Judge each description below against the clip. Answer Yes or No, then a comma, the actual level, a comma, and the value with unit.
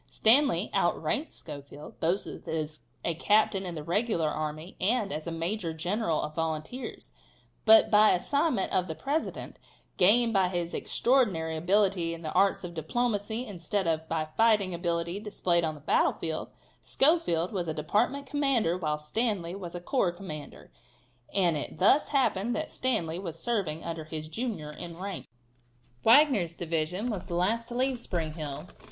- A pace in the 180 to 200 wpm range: No, average, 160 wpm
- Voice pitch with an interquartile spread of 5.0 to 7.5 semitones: Yes, average, 5.3 semitones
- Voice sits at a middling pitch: Yes, medium, 180 Hz